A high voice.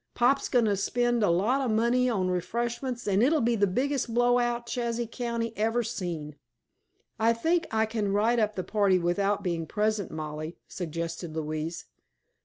Yes: high, 220 Hz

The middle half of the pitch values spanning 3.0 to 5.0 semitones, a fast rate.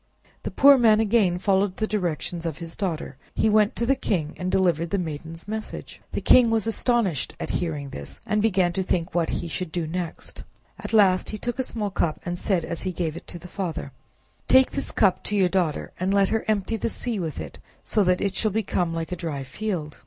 Yes: average, 4.2 semitones; fast, 225 wpm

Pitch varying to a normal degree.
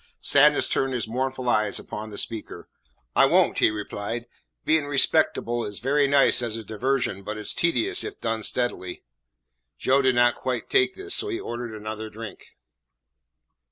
Yes: average, 4.2 semitones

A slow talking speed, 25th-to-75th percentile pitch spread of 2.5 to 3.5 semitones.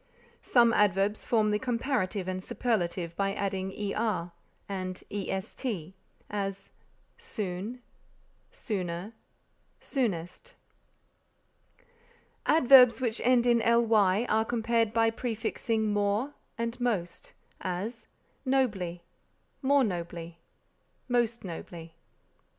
No: slow, 90 wpm; average, 4.1 semitones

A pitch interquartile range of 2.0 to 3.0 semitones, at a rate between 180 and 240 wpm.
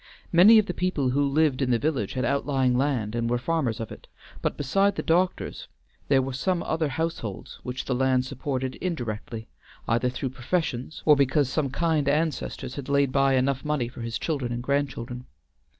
No: average, 3.5 semitones; average, 185 wpm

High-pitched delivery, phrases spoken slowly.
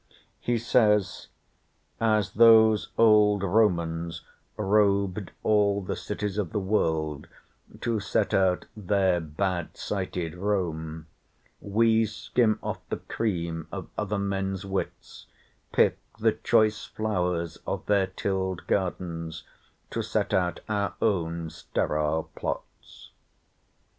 No: very low, 95 Hz; slow, 110 wpm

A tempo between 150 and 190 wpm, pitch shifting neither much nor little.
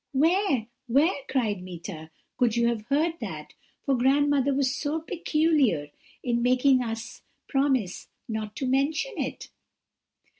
No: slow, 135 wpm; average, 4.2 semitones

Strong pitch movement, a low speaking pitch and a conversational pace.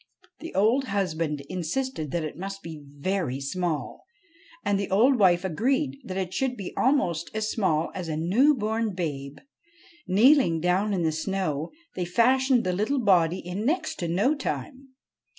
No: wide, 5.9 semitones; high, 190 Hz; average, 165 wpm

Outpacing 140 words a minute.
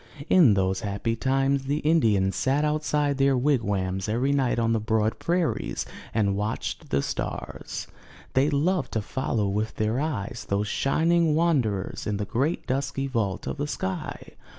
Yes: average, 155 wpm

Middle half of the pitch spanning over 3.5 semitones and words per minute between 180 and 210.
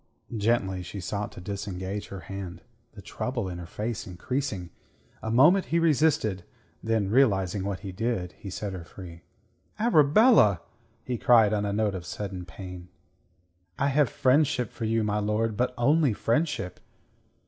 No: average, 5.0 semitones; average, 155 wpm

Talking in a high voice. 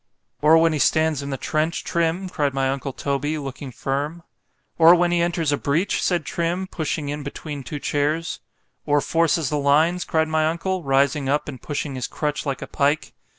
No: medium, 150 Hz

